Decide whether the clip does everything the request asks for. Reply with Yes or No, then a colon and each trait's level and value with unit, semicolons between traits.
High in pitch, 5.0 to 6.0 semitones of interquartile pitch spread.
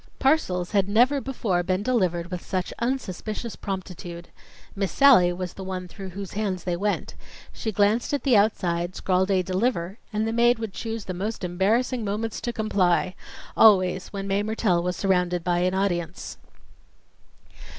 No: high, 195 Hz; average, 3.6 semitones